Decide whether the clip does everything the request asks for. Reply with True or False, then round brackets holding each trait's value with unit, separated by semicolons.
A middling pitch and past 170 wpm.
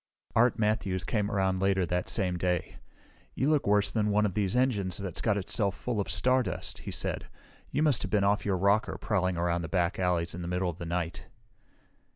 False (100 Hz; 200 wpm)